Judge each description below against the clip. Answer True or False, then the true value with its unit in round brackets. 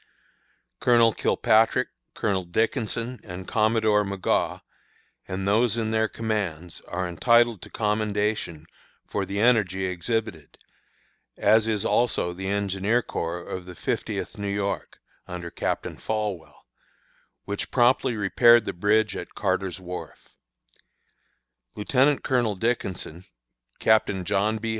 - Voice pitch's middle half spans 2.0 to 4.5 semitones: True (3.2 semitones)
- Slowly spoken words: True (115 wpm)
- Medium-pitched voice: False (105 Hz)